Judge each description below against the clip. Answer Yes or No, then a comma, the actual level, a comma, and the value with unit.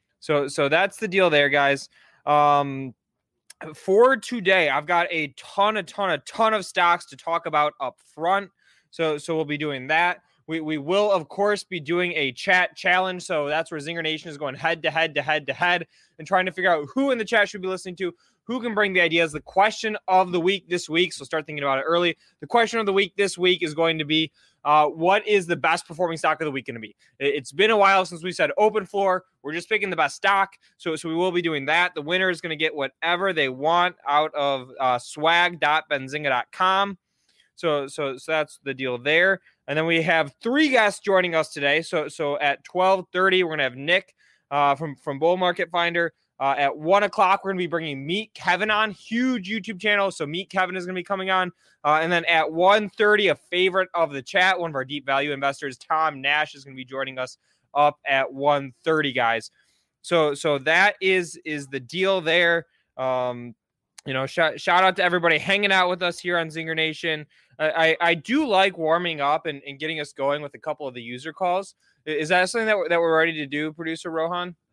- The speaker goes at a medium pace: No, fast, 225 wpm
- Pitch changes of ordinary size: Yes, average, 4.1 semitones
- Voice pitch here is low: No, medium, 165 Hz